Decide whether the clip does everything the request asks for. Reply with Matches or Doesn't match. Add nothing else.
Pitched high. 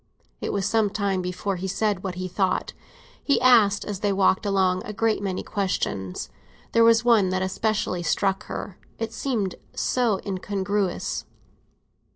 Matches